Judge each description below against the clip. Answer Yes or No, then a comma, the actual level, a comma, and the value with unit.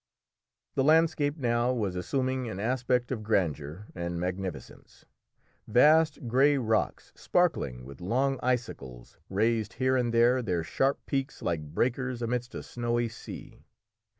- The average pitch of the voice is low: Yes, low, 120 Hz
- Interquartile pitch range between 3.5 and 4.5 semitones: No, wide, 5.5 semitones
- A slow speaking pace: Yes, slow, 130 wpm